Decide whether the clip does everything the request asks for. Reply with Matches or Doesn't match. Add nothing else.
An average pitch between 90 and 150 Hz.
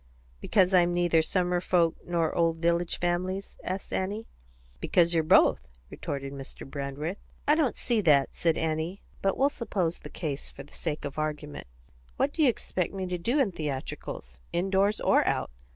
Doesn't match